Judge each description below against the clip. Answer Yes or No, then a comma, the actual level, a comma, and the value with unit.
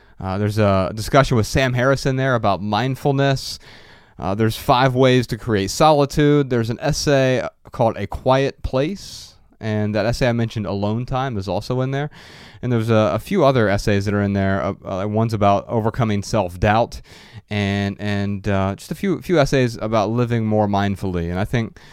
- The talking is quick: No, average, 185 wpm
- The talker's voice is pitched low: Yes, low, 110 Hz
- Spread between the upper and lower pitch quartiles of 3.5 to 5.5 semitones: Yes, average, 4.4 semitones